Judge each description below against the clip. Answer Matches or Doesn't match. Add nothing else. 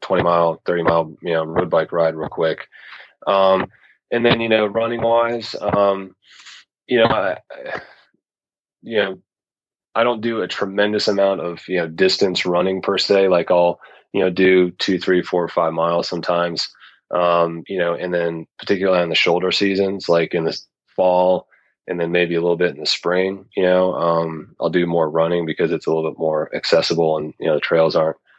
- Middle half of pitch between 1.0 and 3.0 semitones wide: Matches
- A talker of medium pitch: Doesn't match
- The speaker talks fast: Doesn't match